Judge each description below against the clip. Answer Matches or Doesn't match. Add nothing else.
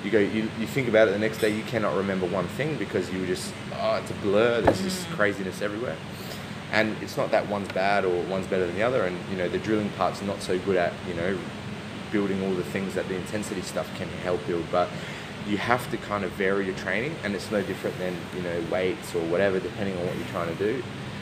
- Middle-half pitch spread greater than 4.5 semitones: Doesn't match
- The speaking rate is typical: Doesn't match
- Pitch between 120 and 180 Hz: Doesn't match